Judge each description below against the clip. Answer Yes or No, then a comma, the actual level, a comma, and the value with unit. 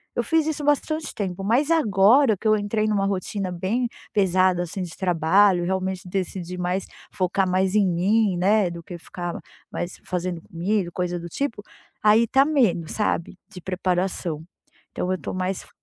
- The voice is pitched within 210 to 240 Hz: No, high, 190 Hz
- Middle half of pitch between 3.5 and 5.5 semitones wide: No, average, 3.1 semitones